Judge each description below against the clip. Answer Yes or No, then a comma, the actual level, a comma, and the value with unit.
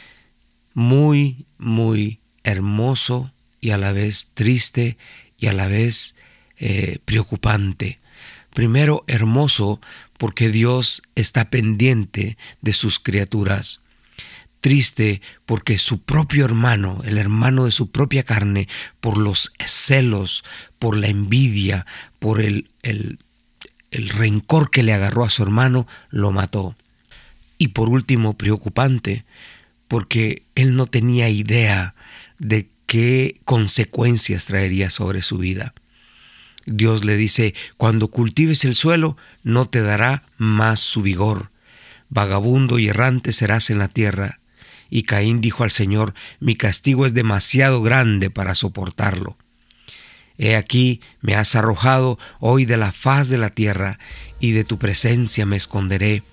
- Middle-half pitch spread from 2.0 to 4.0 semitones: Yes, average, 3.2 semitones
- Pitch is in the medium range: No, low, 110 Hz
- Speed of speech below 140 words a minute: Yes, slow, 125 wpm